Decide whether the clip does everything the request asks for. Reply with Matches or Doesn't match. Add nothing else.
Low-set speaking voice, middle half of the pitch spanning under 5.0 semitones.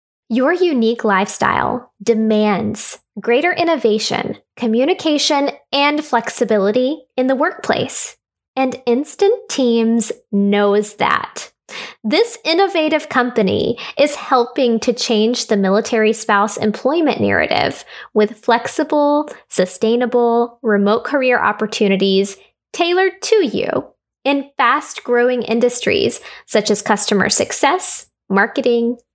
Doesn't match